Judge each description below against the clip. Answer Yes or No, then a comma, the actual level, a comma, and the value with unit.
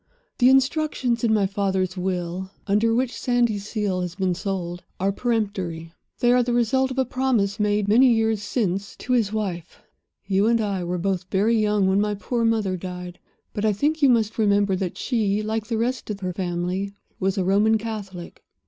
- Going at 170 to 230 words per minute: Yes, average, 185 wpm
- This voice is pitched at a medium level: No, high, 205 Hz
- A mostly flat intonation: No, average, 3.3 semitones